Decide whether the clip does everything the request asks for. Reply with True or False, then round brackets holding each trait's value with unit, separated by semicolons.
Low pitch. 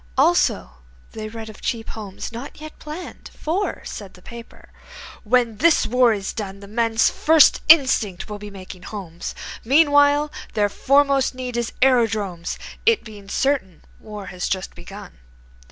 False (225 Hz)